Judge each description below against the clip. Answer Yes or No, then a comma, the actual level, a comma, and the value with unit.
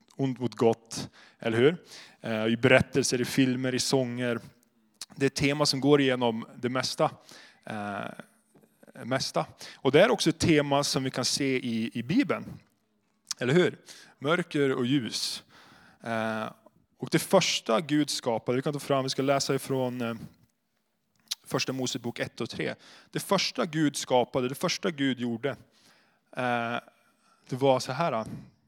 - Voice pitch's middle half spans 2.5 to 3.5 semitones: Yes, average, 3.1 semitones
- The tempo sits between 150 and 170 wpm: No, average, 140 wpm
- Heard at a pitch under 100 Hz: No, low, 130 Hz